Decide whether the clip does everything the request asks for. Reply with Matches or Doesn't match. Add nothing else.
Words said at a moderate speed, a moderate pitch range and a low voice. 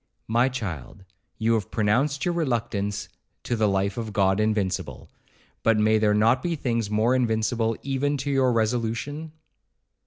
Matches